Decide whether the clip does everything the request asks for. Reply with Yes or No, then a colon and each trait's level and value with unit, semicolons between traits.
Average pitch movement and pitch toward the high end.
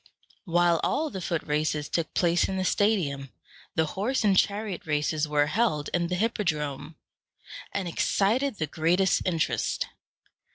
No: average, 4.6 semitones; medium, 175 Hz